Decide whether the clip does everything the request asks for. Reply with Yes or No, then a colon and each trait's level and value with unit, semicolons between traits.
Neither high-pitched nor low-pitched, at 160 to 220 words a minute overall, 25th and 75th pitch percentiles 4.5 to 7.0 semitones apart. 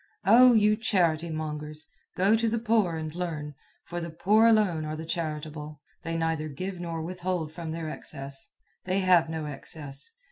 No: medium, 165 Hz; average, 170 wpm; average, 3.2 semitones